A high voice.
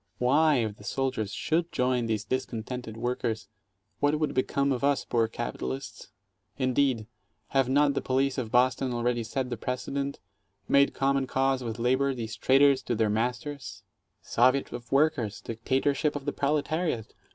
No: low, 130 Hz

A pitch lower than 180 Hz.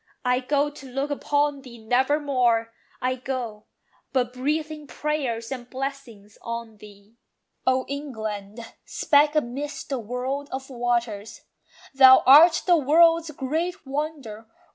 No: very high, 260 Hz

